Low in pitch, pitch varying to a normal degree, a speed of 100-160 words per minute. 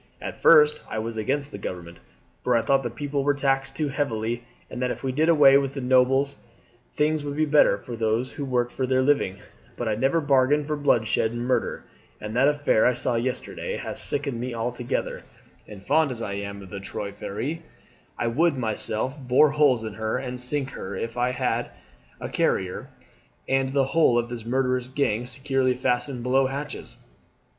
No: low, 130 Hz; average, 3.3 semitones; average, 190 wpm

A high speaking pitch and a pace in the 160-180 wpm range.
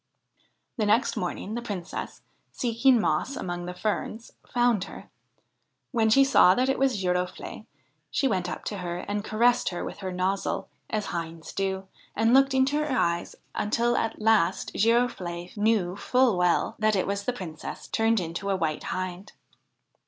Yes: high, 205 Hz; average, 165 wpm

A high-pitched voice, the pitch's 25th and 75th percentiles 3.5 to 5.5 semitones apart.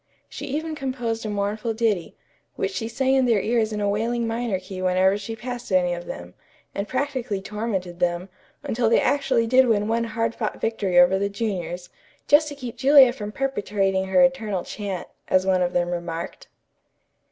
Yes: high, 215 Hz; average, 4.2 semitones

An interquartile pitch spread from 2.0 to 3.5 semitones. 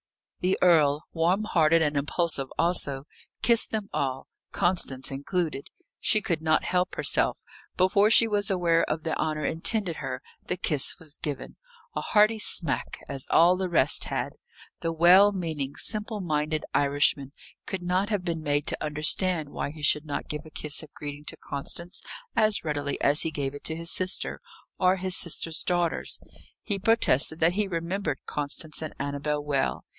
No: average, 3.9 semitones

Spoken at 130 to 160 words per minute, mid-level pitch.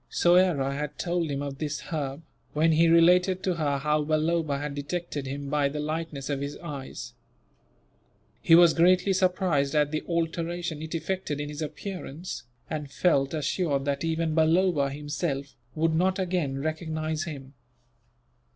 Yes: average, 150 wpm; medium, 155 Hz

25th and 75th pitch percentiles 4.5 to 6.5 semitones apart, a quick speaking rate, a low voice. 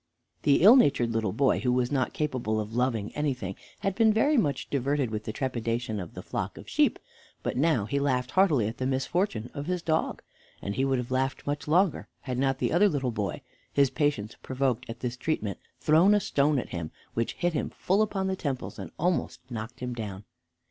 Yes: average, 5.1 semitones; fast, 210 wpm; low, 130 Hz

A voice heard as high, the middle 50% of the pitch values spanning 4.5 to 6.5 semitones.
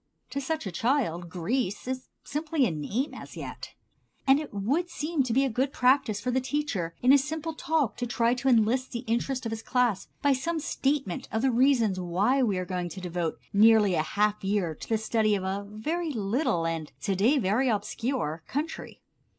Yes: high, 235 Hz; wide, 5.4 semitones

